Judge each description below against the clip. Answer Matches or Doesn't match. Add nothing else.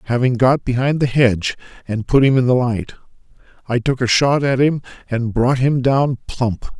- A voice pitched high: Doesn't match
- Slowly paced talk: Doesn't match